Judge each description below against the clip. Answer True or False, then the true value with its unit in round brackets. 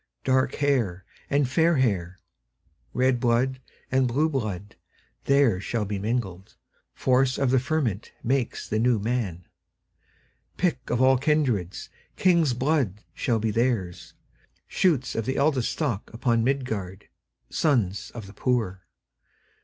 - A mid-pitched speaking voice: False (125 Hz)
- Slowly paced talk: True (100 wpm)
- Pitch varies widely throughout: False (4.3 semitones)